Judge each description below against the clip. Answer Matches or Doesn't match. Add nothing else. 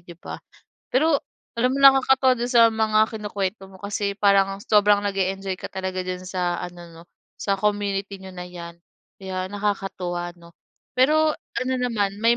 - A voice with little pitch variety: Doesn't match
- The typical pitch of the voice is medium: Doesn't match